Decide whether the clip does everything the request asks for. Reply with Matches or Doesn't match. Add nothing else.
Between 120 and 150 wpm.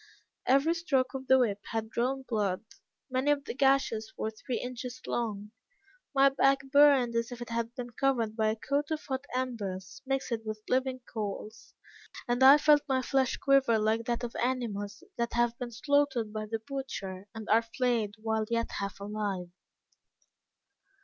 Doesn't match